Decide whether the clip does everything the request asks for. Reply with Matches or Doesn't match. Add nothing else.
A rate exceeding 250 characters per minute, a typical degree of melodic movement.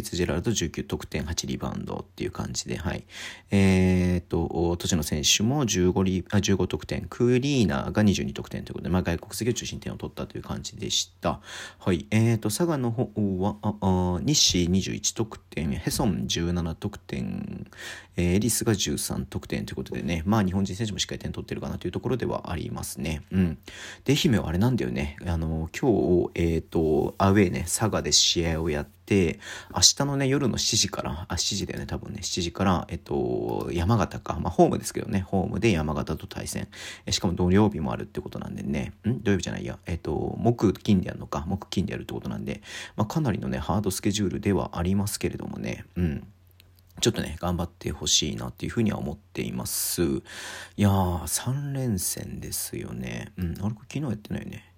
Matches